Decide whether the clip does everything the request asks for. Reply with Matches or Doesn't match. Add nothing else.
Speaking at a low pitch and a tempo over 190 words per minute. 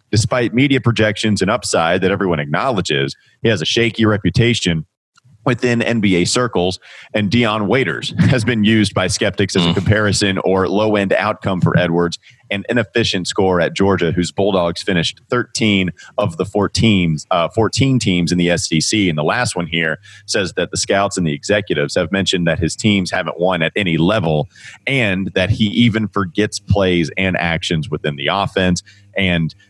Doesn't match